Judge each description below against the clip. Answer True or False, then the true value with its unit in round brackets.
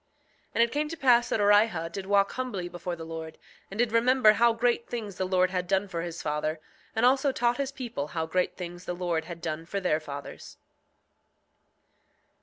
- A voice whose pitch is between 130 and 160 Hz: False (190 Hz)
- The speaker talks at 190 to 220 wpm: True (205 wpm)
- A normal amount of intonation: False (5.8 semitones)